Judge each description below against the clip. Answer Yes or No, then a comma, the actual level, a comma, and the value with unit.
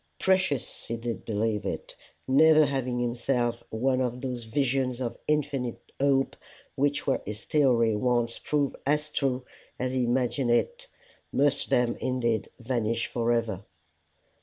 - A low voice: Yes, low, 125 Hz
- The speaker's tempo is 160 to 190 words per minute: No, slow, 135 wpm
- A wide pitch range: No, average, 2.8 semitones